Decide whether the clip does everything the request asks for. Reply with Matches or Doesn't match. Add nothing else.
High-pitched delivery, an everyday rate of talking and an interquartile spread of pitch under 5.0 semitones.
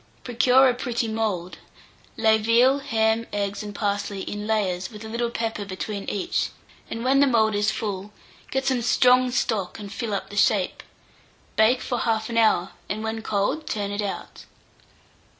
Matches